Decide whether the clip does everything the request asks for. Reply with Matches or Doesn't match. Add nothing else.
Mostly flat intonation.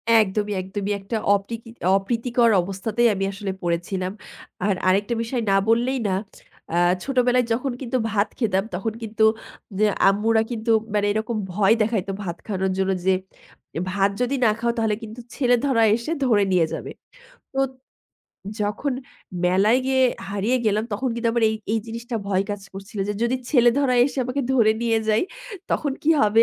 Doesn't match